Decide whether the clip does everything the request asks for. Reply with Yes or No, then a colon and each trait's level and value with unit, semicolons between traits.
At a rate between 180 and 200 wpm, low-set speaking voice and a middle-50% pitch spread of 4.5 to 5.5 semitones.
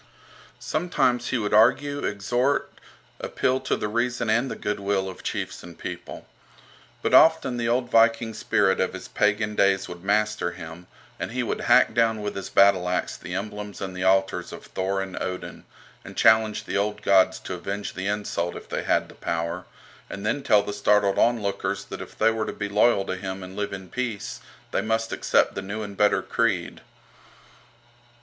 No: average, 185 wpm; low, 105 Hz; average, 2.9 semitones